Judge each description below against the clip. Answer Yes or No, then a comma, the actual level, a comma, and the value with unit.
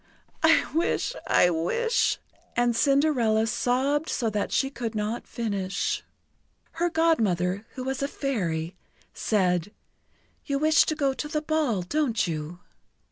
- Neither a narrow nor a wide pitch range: No, wide, 6.9 semitones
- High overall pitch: Yes, high, 240 Hz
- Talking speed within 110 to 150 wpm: Yes, slow, 135 wpm